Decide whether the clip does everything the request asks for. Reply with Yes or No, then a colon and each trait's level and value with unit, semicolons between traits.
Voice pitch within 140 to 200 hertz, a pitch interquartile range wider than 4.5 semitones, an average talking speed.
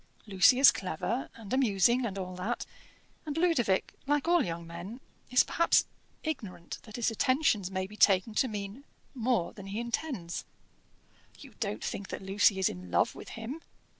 No: high, 215 Hz; average, 5.3 semitones; average, 170 wpm